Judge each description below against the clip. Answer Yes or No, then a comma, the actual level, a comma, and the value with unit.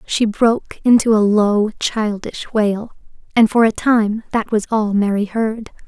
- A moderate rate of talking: Yes, average, 165 wpm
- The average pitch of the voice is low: No, high, 215 Hz